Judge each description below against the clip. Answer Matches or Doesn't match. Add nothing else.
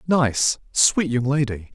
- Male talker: Matches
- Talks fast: Doesn't match